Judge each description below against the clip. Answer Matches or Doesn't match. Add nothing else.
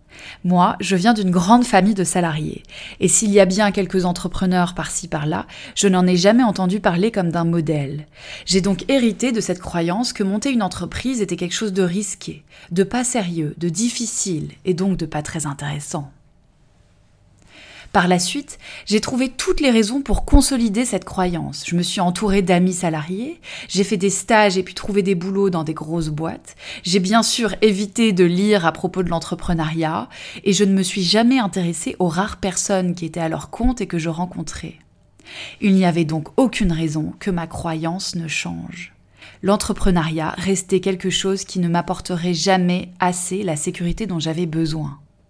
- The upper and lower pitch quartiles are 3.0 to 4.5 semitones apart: Matches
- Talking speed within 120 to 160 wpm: Doesn't match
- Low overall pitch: Doesn't match